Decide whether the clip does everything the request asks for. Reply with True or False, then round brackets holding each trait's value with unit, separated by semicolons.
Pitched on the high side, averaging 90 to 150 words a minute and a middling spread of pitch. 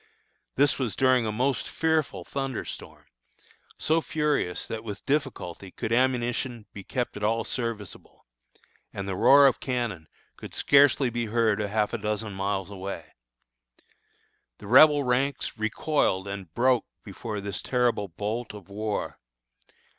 False (115 Hz; 140 wpm; 4.3 semitones)